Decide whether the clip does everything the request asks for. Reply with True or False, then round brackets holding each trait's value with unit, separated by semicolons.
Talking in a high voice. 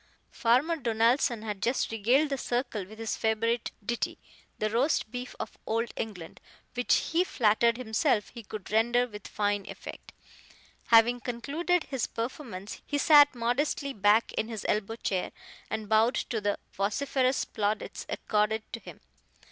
True (230 Hz)